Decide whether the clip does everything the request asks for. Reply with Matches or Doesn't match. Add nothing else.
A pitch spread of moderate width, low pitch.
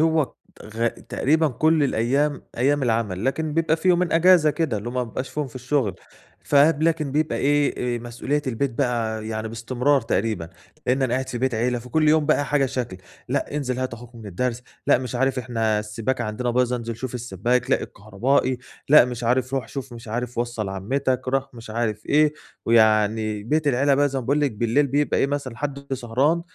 Matches